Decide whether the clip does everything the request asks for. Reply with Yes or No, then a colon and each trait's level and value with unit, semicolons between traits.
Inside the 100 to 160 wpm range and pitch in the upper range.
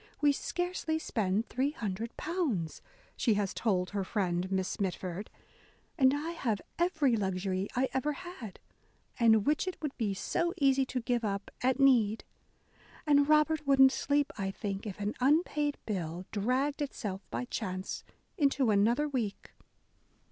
Yes: average, 140 wpm; high, 240 Hz